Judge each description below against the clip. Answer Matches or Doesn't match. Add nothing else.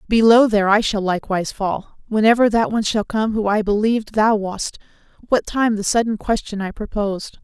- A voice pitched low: Doesn't match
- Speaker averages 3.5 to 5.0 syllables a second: Doesn't match